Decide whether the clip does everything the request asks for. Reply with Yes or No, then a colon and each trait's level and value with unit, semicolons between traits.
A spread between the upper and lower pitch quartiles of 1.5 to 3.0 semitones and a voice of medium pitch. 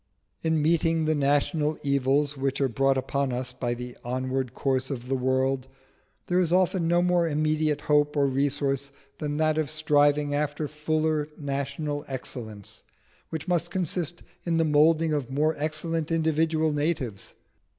Yes: average, 2.7 semitones; medium, 150 Hz